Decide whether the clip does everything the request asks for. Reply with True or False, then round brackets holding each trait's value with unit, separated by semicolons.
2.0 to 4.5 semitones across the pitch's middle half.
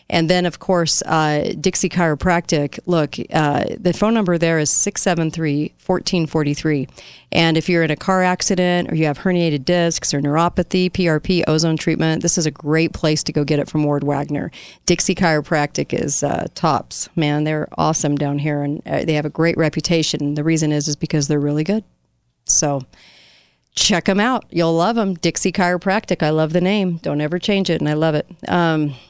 True (3.1 semitones)